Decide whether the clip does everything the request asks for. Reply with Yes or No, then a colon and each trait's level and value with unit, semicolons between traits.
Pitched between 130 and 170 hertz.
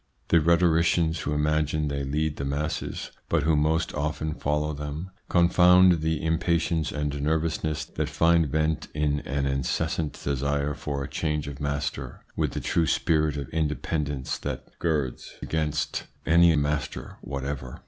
No: very low, 75 Hz